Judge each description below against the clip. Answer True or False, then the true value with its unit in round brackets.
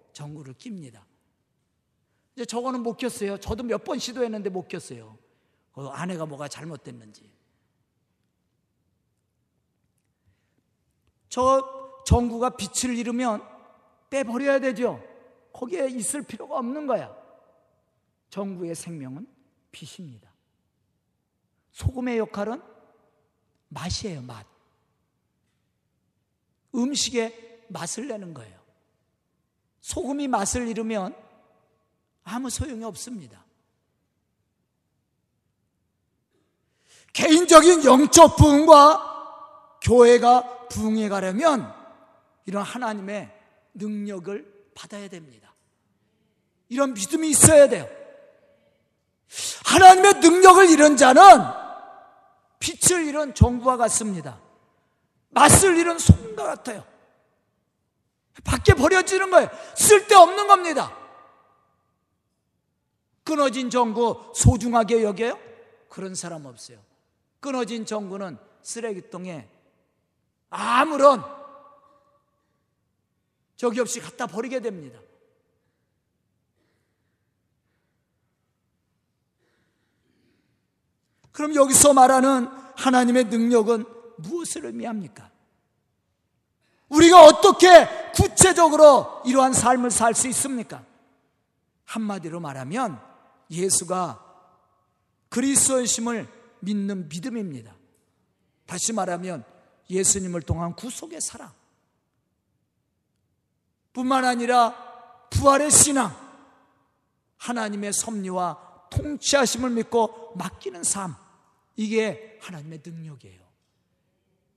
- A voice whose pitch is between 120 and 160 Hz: False (235 Hz)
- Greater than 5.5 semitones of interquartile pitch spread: True (7.3 semitones)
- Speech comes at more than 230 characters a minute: False (195 characters per minute)